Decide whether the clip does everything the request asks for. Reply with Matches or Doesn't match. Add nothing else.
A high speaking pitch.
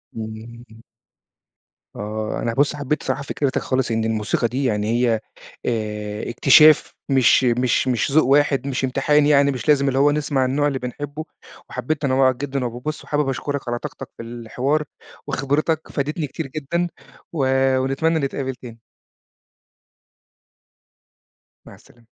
Doesn't match